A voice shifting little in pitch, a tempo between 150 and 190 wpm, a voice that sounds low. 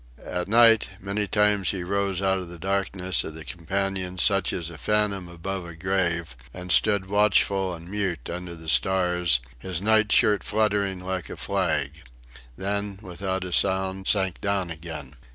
Yes: narrow, 2.3 semitones; average, 165 wpm; very low, 95 Hz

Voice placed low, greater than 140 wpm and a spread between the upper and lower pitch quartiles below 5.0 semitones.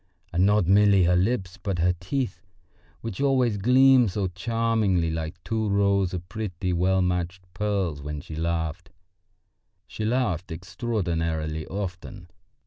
No: very low, 95 Hz; slow, 135 wpm; average, 3.6 semitones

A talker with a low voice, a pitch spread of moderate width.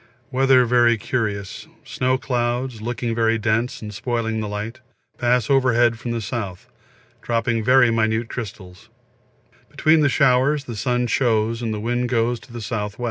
No: low, 120 Hz; narrow, 2.1 semitones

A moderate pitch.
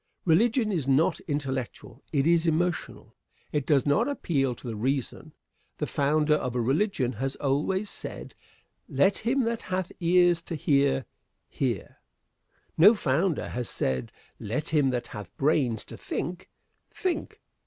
Yes: medium, 150 Hz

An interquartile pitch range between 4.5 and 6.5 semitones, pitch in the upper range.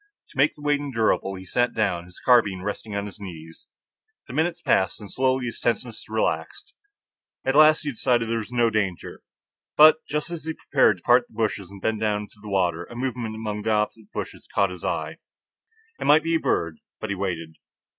No: average, 4.9 semitones; low, 110 Hz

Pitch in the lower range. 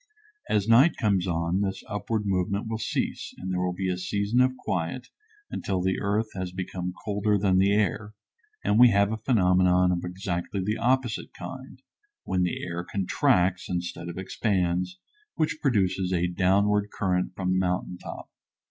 Yes: very low, 95 Hz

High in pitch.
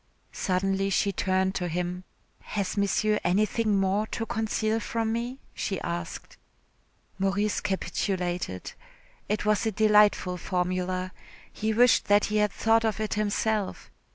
Yes: high, 205 Hz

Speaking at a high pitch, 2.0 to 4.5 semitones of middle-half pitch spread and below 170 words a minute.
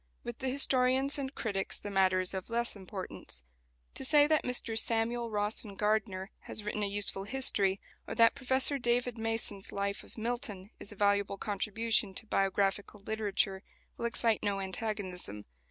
Yes: high, 215 Hz; average, 3.2 semitones; average, 160 wpm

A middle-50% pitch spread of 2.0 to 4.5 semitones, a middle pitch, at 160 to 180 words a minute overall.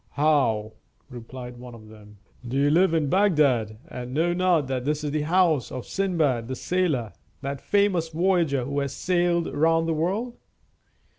No: wide, 5.6 semitones; medium, 150 Hz; average, 165 wpm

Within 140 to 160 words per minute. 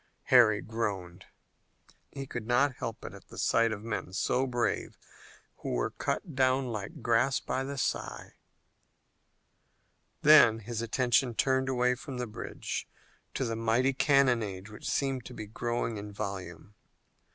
Yes: average, 145 wpm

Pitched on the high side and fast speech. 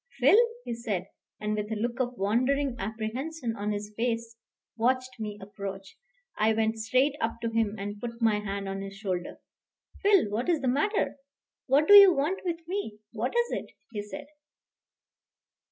No: high, 230 Hz; average, 170 wpm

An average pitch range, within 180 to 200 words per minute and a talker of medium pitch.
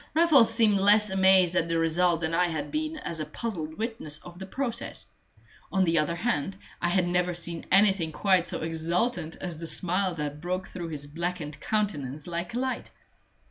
Yes: average, 3.5 semitones; average, 185 wpm; medium, 175 Hz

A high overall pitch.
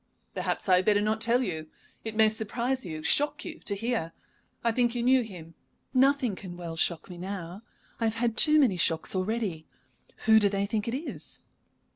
Yes: high, 215 Hz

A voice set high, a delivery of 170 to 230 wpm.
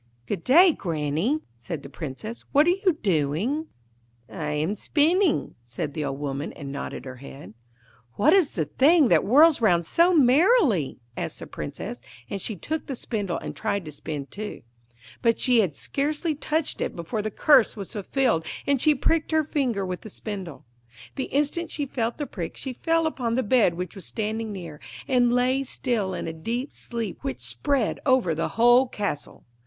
Yes: high, 225 Hz; average, 180 wpm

